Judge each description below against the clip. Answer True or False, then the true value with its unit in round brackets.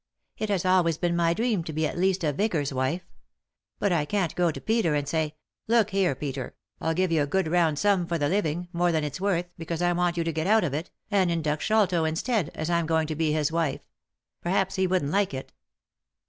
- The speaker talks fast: True (230 wpm)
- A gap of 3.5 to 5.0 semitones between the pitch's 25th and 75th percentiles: False (3.1 semitones)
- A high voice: False (170 Hz)